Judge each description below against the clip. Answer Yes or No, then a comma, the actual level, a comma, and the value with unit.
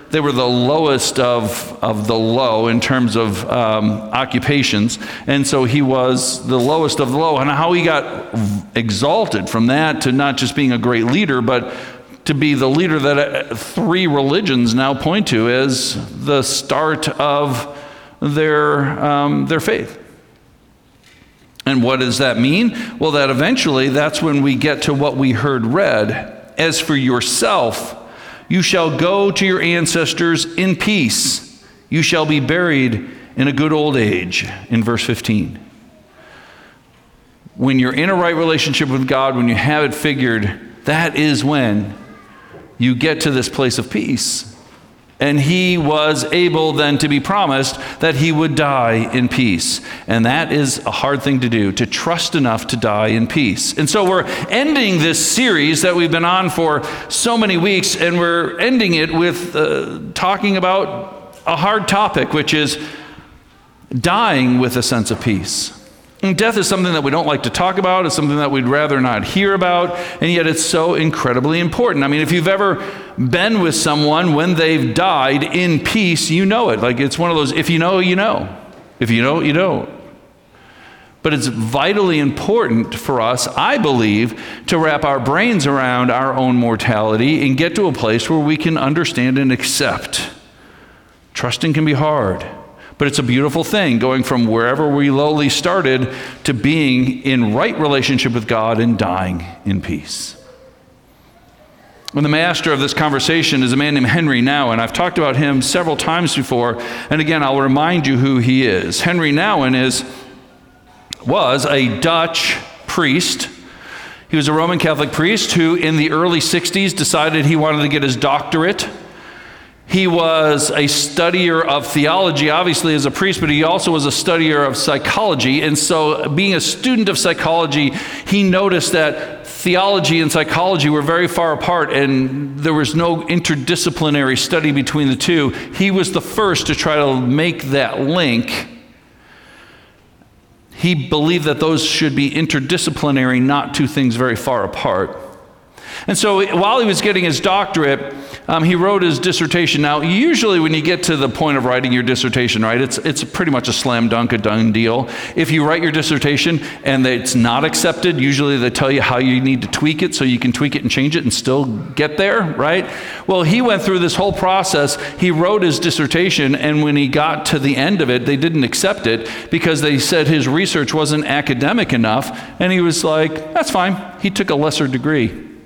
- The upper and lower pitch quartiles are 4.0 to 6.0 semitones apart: Yes, average, 4.4 semitones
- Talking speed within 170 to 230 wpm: Yes, average, 175 wpm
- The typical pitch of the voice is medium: Yes, medium, 150 Hz